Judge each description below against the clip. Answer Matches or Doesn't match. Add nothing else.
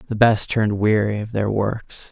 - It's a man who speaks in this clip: Matches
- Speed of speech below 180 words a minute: Doesn't match